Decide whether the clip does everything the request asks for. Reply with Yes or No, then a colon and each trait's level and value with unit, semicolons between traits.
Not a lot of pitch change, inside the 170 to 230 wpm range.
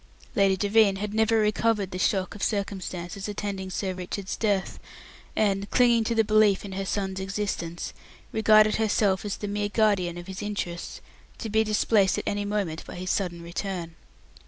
Yes: narrow, 2.1 semitones; average, 175 wpm